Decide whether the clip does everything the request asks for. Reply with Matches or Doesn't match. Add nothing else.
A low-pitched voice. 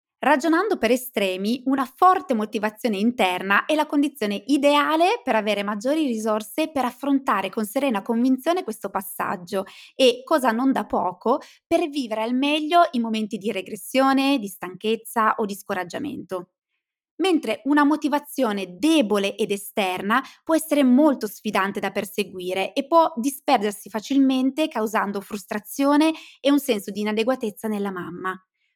Doesn't match